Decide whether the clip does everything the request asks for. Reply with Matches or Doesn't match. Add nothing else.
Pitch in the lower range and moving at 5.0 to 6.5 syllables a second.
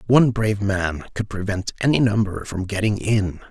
Matches